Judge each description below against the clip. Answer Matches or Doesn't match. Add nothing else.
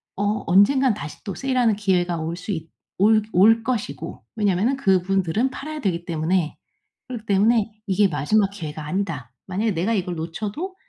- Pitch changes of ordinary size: Matches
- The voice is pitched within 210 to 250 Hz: Doesn't match